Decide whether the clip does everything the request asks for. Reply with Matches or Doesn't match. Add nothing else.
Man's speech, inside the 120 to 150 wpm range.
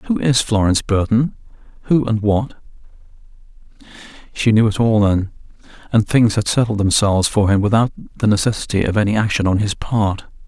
Doesn't match